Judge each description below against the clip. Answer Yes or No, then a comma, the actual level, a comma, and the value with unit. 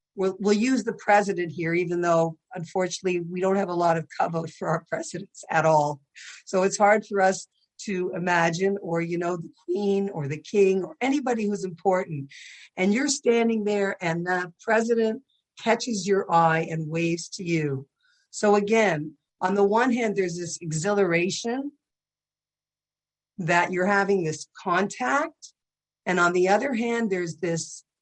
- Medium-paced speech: Yes, average, 160 wpm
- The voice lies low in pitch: No, high, 190 Hz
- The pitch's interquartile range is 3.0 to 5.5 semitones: Yes, average, 3.6 semitones